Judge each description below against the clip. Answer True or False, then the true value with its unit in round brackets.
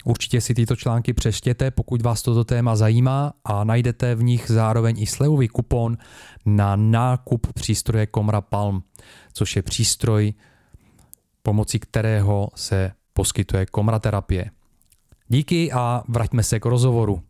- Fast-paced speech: False (130 wpm)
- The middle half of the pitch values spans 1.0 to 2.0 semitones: False (2.5 semitones)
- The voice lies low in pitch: True (115 Hz)